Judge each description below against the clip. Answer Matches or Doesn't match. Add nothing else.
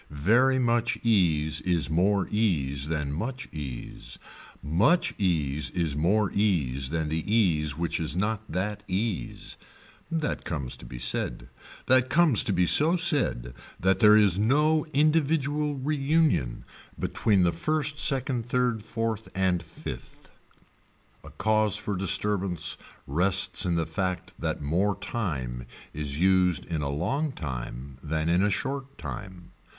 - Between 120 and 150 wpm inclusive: Matches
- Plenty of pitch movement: Matches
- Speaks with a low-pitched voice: Matches